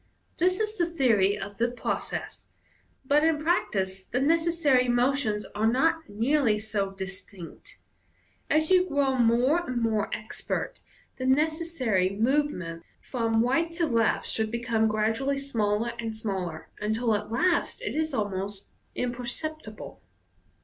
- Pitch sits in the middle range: No, high, 240 Hz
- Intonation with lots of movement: Yes, wide, 5.9 semitones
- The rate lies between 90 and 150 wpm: Yes, slow, 135 wpm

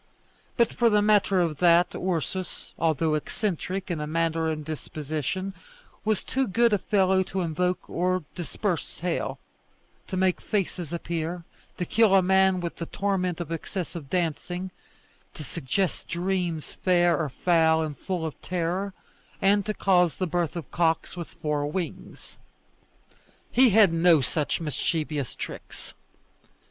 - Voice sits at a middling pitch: Yes, medium, 175 Hz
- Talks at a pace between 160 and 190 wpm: No, average, 140 wpm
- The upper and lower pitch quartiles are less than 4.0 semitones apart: Yes, average, 2.9 semitones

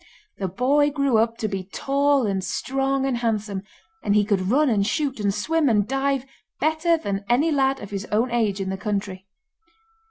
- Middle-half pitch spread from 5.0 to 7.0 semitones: Yes, average, 5.3 semitones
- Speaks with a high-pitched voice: Yes, high, 230 Hz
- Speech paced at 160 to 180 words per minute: No, average, 190 wpm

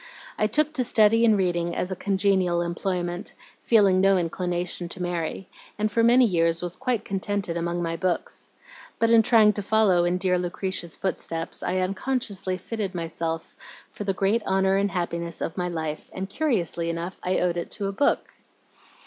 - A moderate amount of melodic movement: Yes, average, 3.0 semitones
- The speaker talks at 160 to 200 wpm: Yes, average, 175 wpm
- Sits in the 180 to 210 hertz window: Yes, medium, 185 Hz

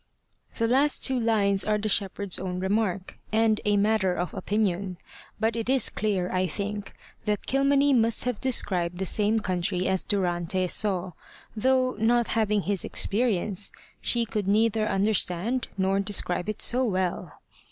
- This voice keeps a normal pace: Yes, average, 150 wpm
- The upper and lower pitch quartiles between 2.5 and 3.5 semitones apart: Yes, average, 3.1 semitones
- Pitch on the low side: No, high, 205 Hz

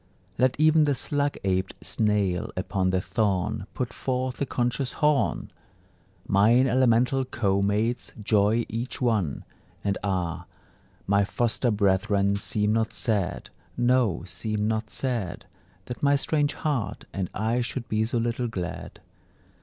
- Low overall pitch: Yes, low, 110 Hz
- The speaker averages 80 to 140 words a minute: Yes, slow, 135 wpm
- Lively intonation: No, average, 4.2 semitones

